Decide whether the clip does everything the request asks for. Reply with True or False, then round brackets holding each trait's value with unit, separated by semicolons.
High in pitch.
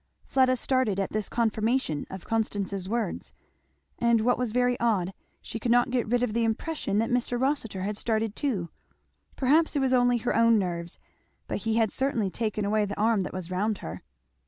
True (225 Hz)